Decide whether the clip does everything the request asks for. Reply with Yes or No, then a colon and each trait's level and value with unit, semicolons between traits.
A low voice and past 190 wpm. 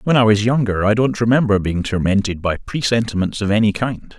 Yes: low, 110 Hz; average, 200 wpm